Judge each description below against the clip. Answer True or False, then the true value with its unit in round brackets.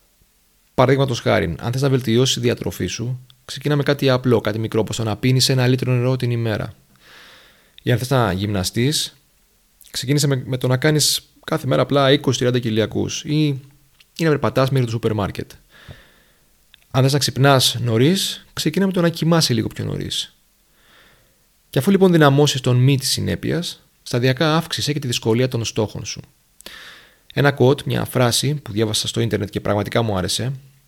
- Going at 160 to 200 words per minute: True (170 wpm)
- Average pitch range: True (3.9 semitones)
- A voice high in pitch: False (130 Hz)